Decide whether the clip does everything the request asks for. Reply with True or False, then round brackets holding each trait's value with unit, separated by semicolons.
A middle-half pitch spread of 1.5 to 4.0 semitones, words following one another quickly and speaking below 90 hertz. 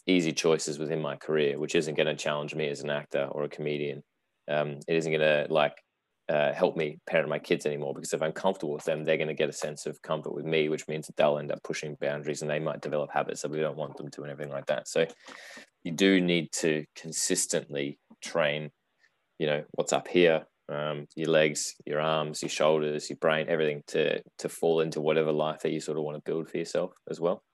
False (1.1 semitones; 235 wpm; 75 Hz)